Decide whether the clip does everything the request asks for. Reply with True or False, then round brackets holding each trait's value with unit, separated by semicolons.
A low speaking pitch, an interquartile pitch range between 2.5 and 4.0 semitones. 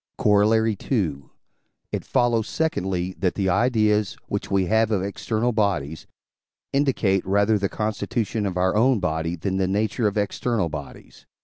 True (100 Hz; 3.1 semitones)